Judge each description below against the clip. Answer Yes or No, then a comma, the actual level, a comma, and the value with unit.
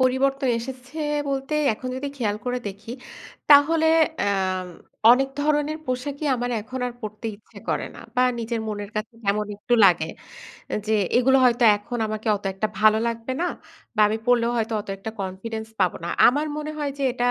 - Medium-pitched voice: No, high, 240 Hz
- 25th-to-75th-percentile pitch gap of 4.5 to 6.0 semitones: No, average, 3.9 semitones